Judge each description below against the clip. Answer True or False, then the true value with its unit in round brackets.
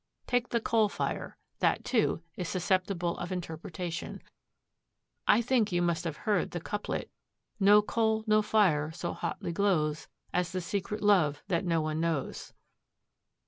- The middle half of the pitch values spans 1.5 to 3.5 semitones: False (3.9 semitones)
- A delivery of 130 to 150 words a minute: True (145 wpm)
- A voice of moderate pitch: True (180 Hz)